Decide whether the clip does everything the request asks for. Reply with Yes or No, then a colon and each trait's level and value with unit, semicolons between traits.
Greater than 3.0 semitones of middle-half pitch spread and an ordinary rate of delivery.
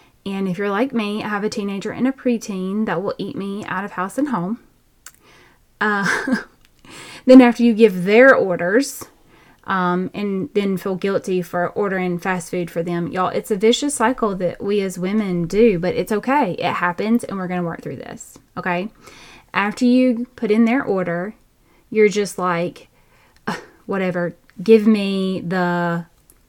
Yes: average, 3.7 semitones; average, 170 wpm